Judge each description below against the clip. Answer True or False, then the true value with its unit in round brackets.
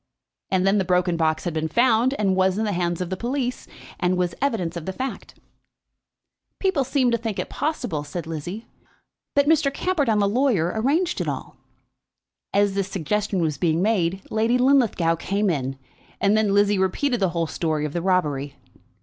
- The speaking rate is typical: True (185 wpm)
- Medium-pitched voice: False (195 Hz)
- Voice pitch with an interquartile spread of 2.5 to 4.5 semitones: False (5.6 semitones)